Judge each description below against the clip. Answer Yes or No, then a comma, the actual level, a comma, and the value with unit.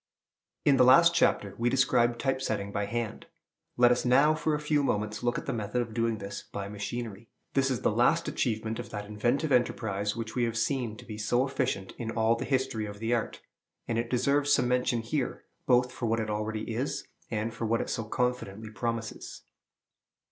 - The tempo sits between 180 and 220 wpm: Yes, fast, 205 wpm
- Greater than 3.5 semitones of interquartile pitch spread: No, average, 2.7 semitones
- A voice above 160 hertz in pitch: No, low, 115 Hz